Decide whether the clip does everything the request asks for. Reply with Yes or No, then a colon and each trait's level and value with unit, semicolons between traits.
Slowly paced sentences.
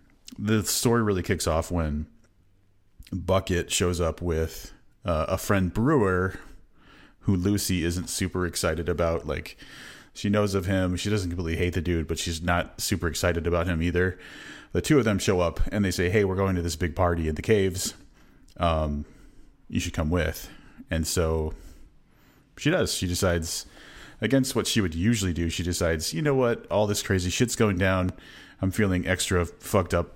No: average, 180 wpm